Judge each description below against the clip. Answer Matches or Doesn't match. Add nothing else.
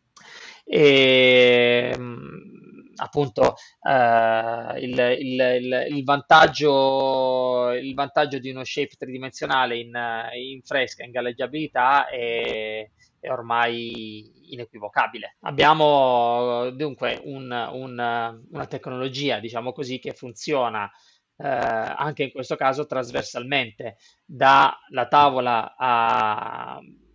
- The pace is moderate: Doesn't match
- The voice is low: Matches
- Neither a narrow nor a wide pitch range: Doesn't match